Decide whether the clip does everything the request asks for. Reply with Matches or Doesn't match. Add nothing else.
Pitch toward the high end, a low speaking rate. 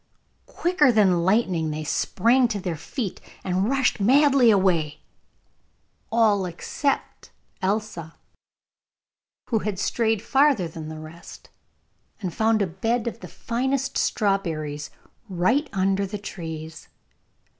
Matches